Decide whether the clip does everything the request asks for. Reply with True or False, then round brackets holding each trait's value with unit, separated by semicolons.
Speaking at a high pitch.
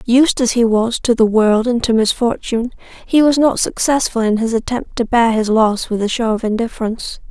True (235 Hz)